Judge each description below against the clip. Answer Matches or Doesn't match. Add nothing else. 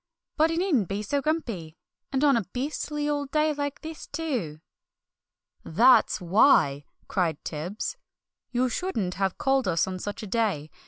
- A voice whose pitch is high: Matches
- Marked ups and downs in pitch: Matches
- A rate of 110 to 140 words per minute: Doesn't match